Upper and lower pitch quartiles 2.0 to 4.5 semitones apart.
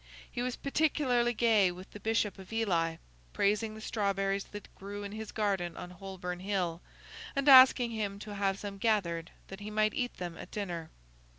Yes: average, 2.9 semitones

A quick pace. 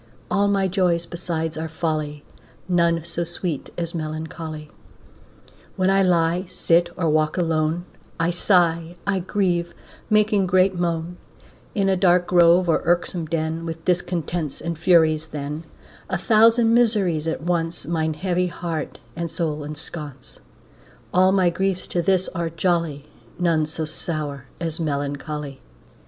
No: average, 140 wpm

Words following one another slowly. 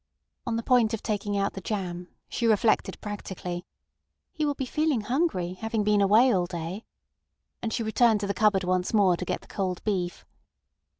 No: average, 185 wpm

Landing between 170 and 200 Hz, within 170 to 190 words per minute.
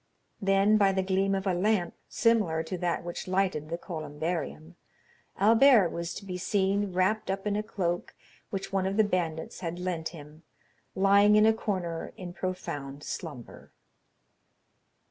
No: medium, 185 Hz; average, 155 wpm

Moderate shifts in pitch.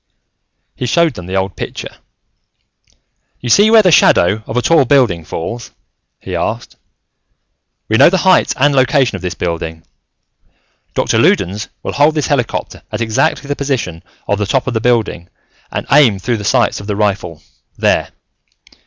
No: wide, 6.5 semitones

